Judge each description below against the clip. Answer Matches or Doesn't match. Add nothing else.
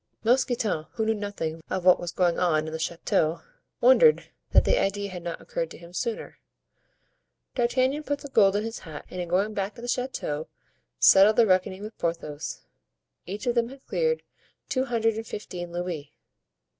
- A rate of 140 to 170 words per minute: Doesn't match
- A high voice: Matches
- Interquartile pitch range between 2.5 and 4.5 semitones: Doesn't match